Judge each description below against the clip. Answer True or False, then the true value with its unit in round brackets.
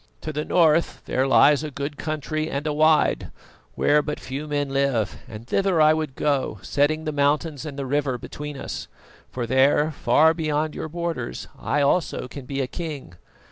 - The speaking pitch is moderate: True (145 Hz)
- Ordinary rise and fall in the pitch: False (2.2 semitones)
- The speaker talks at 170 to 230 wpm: True (180 wpm)